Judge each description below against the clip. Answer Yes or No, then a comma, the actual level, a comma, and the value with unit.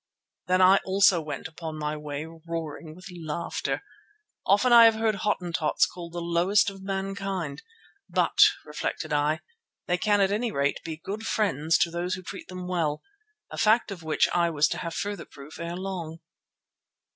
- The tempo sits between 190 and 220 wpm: No, average, 170 wpm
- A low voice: No, medium, 175 Hz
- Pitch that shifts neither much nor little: Yes, average, 3.7 semitones